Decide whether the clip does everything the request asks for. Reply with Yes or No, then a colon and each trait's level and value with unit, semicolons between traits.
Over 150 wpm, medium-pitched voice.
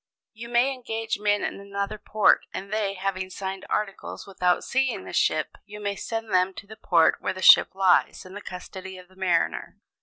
No: average, 195 wpm; high, 200 Hz